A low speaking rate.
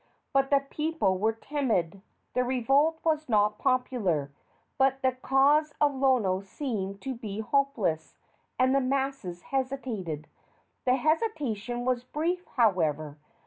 Yes: slow, 125 wpm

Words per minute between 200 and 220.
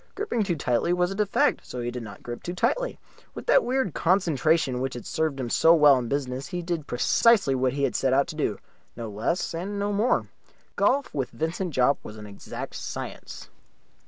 Yes: fast, 205 wpm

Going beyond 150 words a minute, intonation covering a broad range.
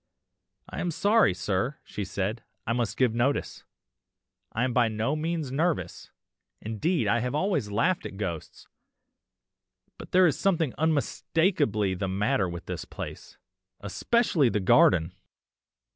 No: slow, 135 wpm; wide, 7.7 semitones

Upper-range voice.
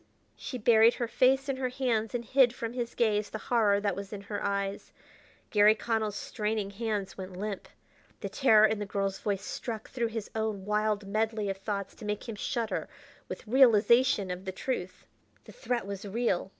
Yes: high, 215 Hz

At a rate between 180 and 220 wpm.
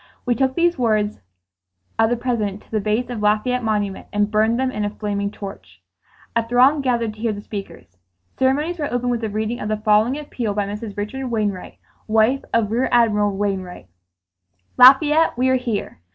Yes: average, 185 wpm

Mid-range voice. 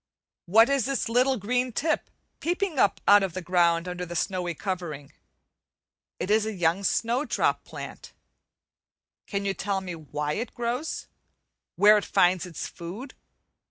No: high, 200 Hz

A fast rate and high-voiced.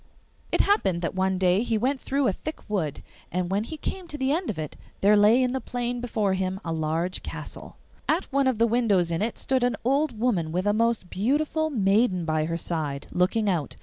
Yes: fast, 220 wpm; high, 210 Hz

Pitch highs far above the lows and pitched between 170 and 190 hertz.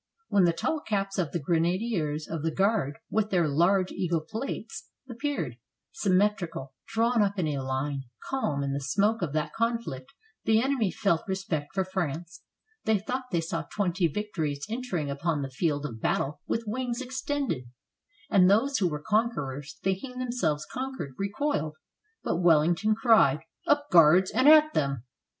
Yes: wide, 6.7 semitones; medium, 185 Hz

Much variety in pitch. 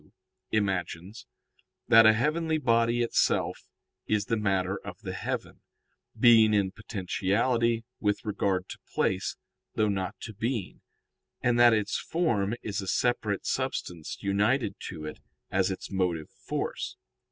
No: average, 3.4 semitones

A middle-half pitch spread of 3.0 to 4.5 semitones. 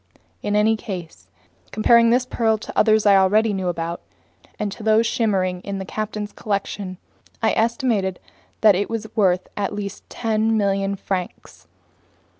No: narrow, 2.4 semitones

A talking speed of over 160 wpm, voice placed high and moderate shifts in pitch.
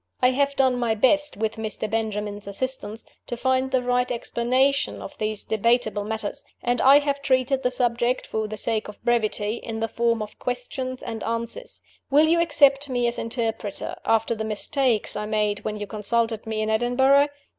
Yes: average, 180 wpm; high, 235 Hz; average, 3.1 semitones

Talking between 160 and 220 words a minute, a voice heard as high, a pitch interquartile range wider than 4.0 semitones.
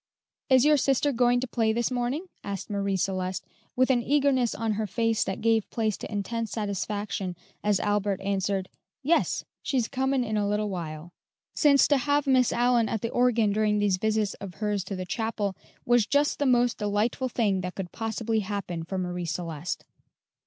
No: average, 180 wpm; high, 215 Hz; average, 3.7 semitones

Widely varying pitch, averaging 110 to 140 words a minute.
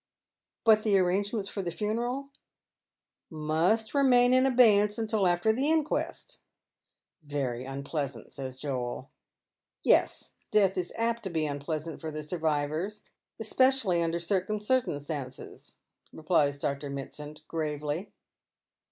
Yes: wide, 6.8 semitones; slow, 135 wpm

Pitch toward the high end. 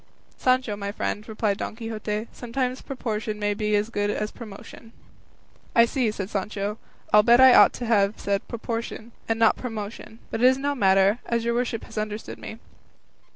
Yes: high, 220 Hz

